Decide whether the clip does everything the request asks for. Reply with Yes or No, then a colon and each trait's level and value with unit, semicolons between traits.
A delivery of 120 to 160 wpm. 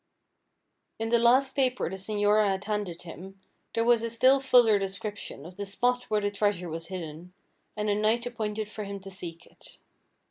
No: average, 185 wpm